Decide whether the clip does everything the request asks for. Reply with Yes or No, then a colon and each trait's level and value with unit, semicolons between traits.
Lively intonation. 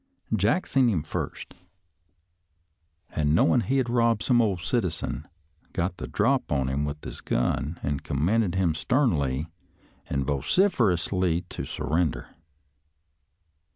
Yes: wide, 7.6 semitones